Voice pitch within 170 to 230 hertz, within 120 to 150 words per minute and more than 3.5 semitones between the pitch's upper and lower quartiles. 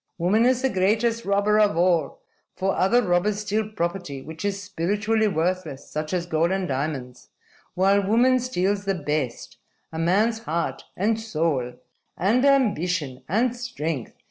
Yes: high, 190 Hz; average, 145 wpm; average, 4.9 semitones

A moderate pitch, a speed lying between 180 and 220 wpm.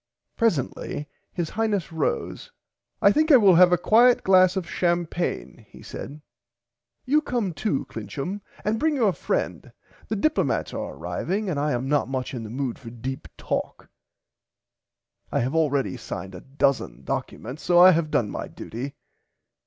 No: medium, 170 Hz; average, 160 wpm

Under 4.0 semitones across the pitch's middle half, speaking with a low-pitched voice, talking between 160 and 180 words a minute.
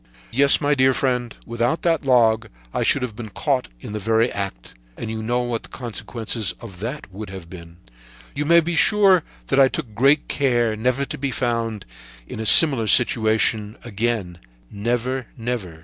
Yes: average, 3.4 semitones; low, 120 Hz; average, 170 wpm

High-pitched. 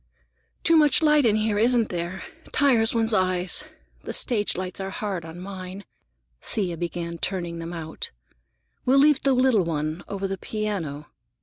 Yes: high, 195 Hz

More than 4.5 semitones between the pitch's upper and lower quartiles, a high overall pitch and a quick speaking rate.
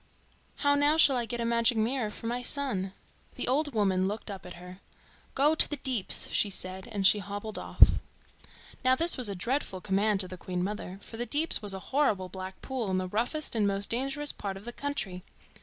Yes: wide, 5.5 semitones; high, 215 Hz; fast, 215 wpm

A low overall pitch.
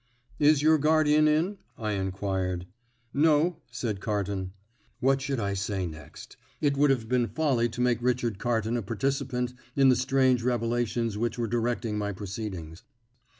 Yes: low, 120 Hz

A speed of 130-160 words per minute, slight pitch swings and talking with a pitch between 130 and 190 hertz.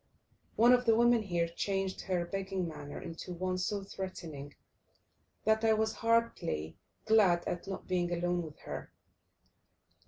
No: average, 145 wpm; average, 4.1 semitones; medium, 185 Hz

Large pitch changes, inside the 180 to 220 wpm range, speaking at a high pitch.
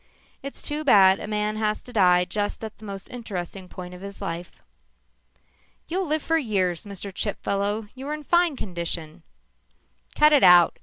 No: wide, 6.0 semitones; average, 165 wpm; high, 205 Hz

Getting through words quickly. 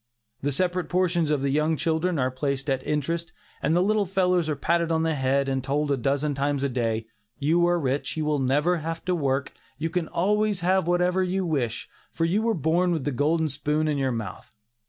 Yes: fast, 220 wpm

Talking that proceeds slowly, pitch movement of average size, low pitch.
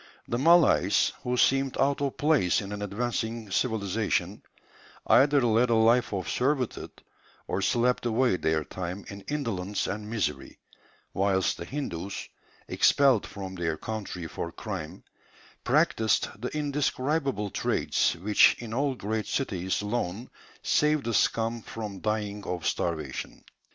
Yes: slow, 130 wpm; average, 4.8 semitones; low, 110 Hz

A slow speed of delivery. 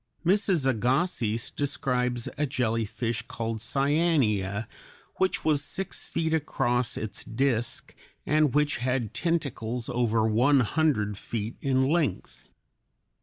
Yes: slow, 110 wpm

